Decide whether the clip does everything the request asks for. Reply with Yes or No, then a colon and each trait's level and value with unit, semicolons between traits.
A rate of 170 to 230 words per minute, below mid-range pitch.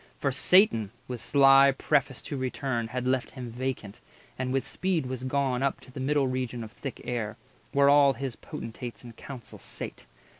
Yes: average, 180 wpm; low, 130 Hz